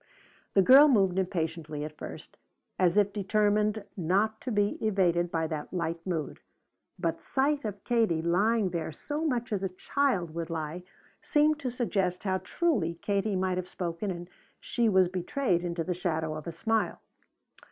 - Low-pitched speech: No, high, 190 Hz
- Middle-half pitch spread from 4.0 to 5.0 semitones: Yes, average, 4.3 semitones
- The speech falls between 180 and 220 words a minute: No, average, 165 wpm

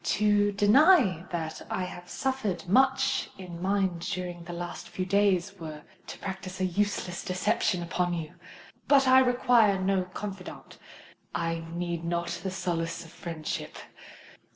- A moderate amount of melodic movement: Yes, average, 3.1 semitones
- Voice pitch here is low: No, medium, 185 Hz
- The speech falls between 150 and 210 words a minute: No, slow, 135 wpm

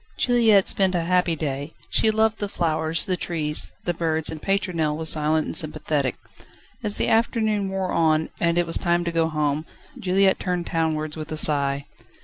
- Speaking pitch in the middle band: Yes, medium, 165 Hz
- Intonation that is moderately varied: Yes, average, 3.5 semitones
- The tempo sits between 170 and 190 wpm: Yes, average, 180 wpm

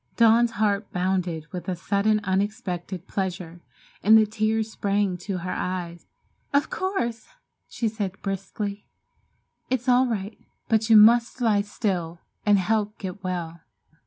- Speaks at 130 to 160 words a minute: Yes, slow, 135 wpm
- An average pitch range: Yes, average, 3.3 semitones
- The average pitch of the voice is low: No, high, 205 Hz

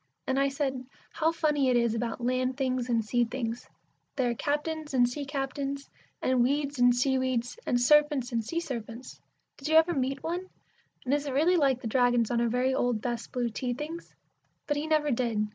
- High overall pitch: Yes, very high, 260 Hz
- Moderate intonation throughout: Yes, average, 3.2 semitones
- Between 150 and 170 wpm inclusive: No, fast, 205 wpm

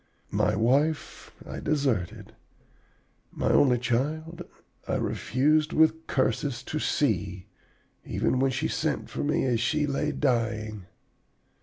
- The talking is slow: Yes, slow, 120 wpm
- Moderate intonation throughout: Yes, average, 4.6 semitones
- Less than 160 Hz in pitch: Yes, low, 135 Hz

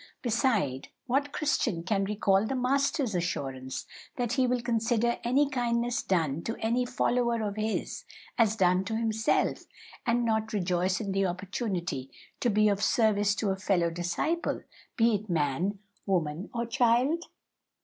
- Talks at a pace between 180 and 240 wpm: No, average, 150 wpm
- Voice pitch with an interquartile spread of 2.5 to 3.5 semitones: No, average, 4.3 semitones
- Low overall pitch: No, high, 220 Hz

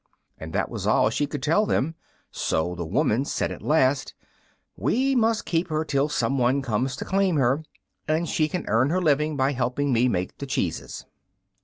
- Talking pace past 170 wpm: Yes, average, 190 wpm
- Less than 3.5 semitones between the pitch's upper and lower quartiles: No, average, 4.3 semitones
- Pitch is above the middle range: No, medium, 140 Hz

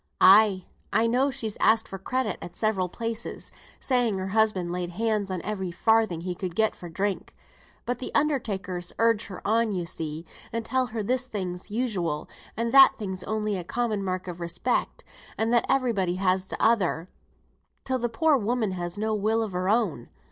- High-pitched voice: Yes, high, 210 Hz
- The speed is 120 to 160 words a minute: No, average, 185 wpm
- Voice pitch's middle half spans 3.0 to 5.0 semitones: Yes, average, 3.9 semitones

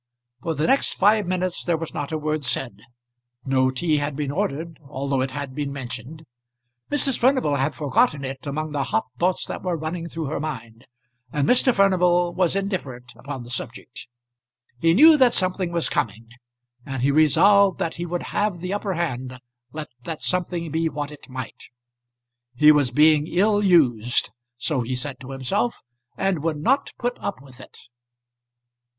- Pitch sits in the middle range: Yes, medium, 155 Hz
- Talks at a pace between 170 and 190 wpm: Yes, average, 175 wpm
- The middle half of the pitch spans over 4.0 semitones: Yes, average, 5.2 semitones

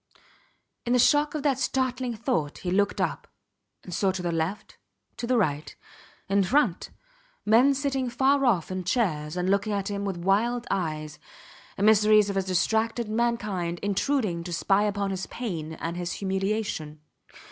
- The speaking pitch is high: Yes, high, 200 Hz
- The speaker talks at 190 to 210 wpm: No, average, 160 wpm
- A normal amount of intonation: Yes, average, 4.9 semitones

